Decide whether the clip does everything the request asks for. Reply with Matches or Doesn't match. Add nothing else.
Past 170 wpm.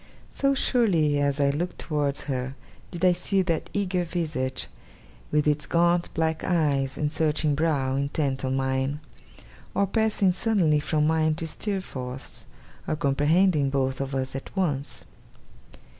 Doesn't match